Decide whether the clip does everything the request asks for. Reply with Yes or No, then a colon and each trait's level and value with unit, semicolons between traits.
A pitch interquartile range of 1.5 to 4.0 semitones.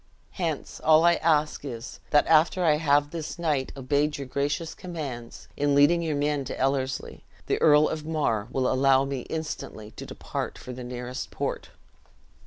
Yes: average, 3.1 semitones